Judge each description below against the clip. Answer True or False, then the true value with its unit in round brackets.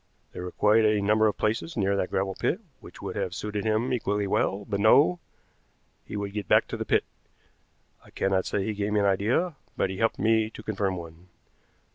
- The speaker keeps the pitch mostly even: True (2.0 semitones)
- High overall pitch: False (105 Hz)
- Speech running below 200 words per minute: False (205 wpm)